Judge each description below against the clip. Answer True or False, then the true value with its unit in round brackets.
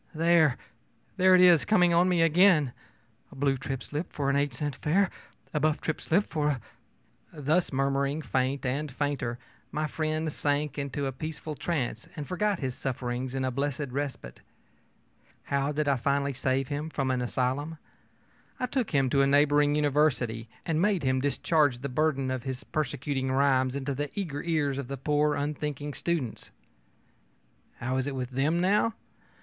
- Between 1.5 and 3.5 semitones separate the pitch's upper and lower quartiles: True (2.8 semitones)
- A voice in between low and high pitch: True (145 Hz)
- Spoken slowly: False (175 wpm)